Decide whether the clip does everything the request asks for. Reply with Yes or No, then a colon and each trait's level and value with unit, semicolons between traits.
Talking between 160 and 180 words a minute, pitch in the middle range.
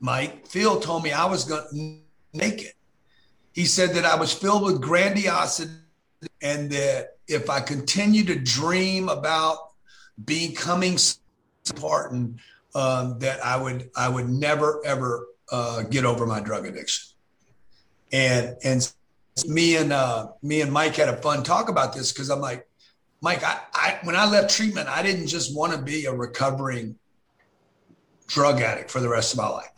Yes: average, 165 wpm; medium, 145 Hz